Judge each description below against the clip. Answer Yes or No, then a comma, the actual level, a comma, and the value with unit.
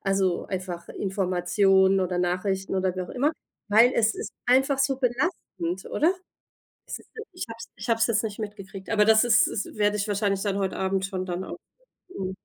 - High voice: Yes, high, 195 Hz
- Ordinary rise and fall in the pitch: Yes, average, 3.2 semitones